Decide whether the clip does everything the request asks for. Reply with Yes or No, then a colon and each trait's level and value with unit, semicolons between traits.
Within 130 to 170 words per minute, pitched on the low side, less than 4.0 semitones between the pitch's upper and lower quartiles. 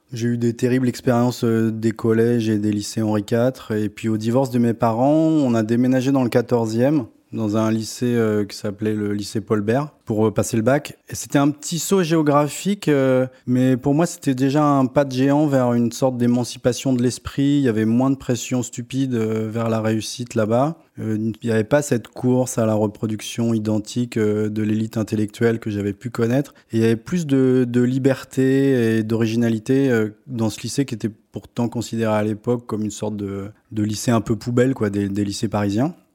No: average, 210 wpm; low, 115 Hz; average, 3.0 semitones